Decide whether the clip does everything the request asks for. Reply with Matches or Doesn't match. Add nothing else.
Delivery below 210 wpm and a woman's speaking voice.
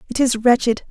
Matches